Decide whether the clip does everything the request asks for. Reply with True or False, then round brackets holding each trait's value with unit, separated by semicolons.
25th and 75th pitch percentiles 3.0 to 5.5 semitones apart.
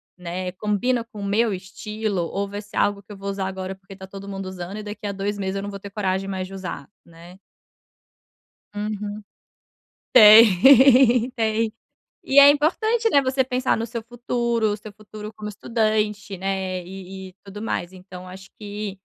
False (2.6 semitones)